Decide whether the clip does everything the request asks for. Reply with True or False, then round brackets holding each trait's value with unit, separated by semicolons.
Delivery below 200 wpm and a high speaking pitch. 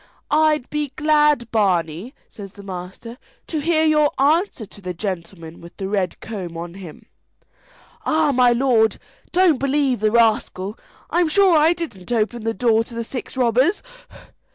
True (155 wpm; 235 Hz)